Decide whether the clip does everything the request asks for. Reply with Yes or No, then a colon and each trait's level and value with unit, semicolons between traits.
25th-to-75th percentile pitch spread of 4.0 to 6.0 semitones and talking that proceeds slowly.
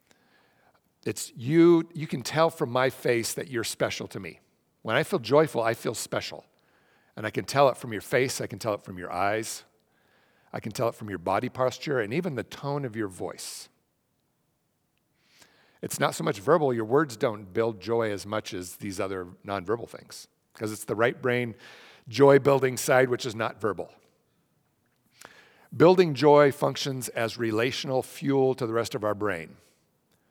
No: average, 4.4 semitones; average, 180 wpm